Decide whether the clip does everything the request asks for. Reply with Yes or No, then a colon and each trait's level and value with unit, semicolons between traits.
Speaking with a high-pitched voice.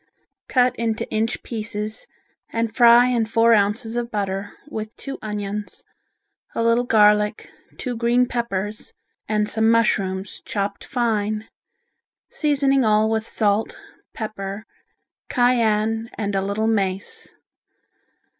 Yes: high, 220 Hz